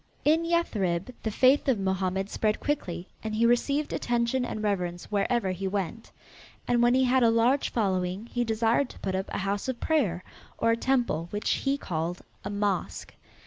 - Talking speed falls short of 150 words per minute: No, average, 185 wpm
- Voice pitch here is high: Yes, high, 220 Hz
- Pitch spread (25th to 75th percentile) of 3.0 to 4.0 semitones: No, average, 4.6 semitones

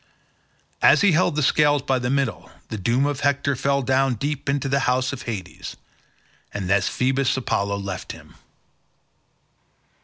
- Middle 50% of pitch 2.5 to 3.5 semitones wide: Yes, average, 3.2 semitones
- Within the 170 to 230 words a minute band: No, average, 150 wpm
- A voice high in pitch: No, low, 130 Hz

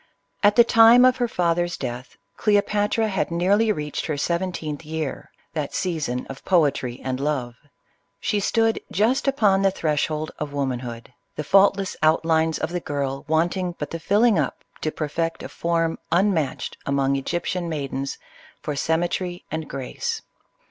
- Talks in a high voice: No, medium, 165 Hz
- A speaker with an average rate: Yes, average, 155 wpm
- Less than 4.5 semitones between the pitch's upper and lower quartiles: No, average, 5.2 semitones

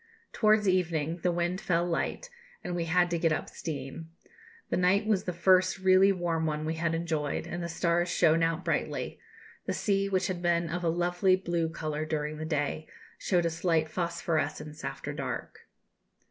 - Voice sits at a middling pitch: Yes, medium, 170 Hz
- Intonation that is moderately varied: No, narrow, 2.0 semitones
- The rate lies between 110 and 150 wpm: No, average, 180 wpm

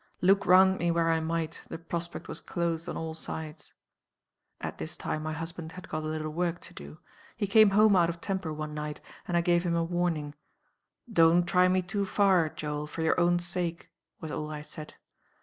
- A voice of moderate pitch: Yes, medium, 170 Hz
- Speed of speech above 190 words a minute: Yes, fast, 205 wpm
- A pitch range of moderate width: No, narrow, 2.2 semitones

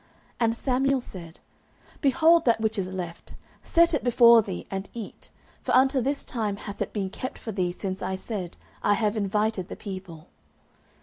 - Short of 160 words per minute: No, average, 175 wpm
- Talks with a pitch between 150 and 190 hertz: No, high, 215 Hz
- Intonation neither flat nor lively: Yes, average, 4.6 semitones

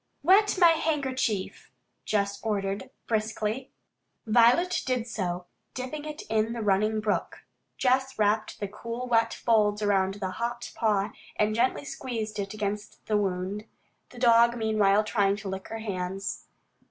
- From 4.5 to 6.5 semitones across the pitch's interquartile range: No, average, 2.9 semitones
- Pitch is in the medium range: No, high, 215 Hz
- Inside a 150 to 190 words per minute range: No, average, 140 wpm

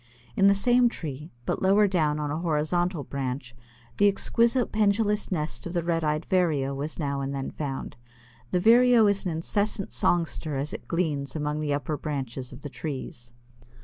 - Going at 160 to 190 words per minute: Yes, average, 180 wpm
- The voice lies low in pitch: No, medium, 155 Hz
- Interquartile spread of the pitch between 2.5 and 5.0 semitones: No, wide, 5.6 semitones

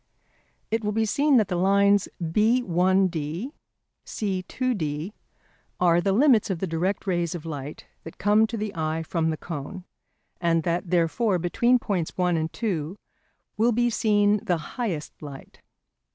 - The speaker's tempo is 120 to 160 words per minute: Yes, average, 150 wpm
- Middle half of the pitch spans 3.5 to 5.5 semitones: Yes, average, 4.5 semitones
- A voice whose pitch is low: No, medium, 185 Hz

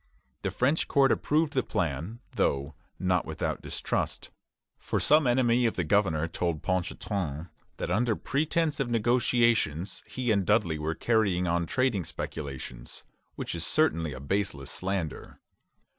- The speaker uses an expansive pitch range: Yes, wide, 6.9 semitones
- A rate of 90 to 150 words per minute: Yes, average, 140 wpm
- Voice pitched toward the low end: Yes, very low, 95 Hz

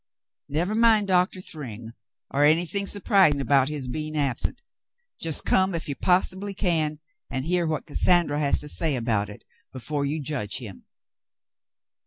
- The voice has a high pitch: No, medium, 155 Hz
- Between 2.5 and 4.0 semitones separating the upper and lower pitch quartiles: No, average, 4.6 semitones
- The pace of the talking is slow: No, average, 150 wpm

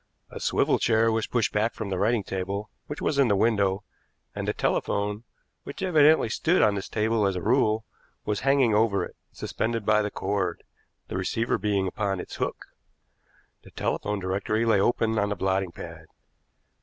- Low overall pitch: Yes, low, 105 Hz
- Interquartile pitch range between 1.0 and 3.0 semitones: Yes, narrow, 2.6 semitones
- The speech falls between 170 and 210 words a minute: Yes, average, 180 wpm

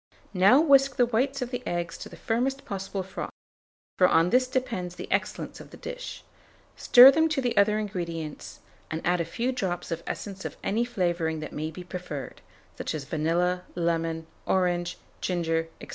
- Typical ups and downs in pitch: No, wide, 6.5 semitones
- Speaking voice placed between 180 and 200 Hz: Yes, medium, 185 Hz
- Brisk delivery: No, average, 180 wpm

